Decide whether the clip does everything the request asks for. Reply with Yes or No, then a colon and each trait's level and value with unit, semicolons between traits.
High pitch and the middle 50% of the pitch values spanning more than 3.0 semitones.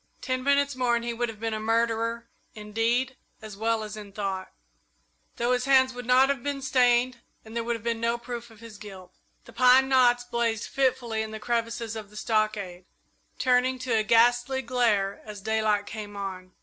No: high, 230 Hz; narrow, 2.5 semitones